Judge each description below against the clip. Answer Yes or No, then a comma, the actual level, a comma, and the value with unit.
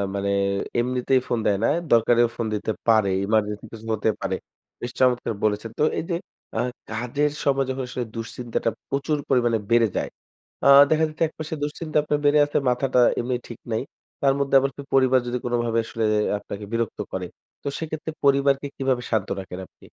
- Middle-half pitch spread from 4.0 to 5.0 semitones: No, average, 3.4 semitones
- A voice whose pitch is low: Yes, low, 125 Hz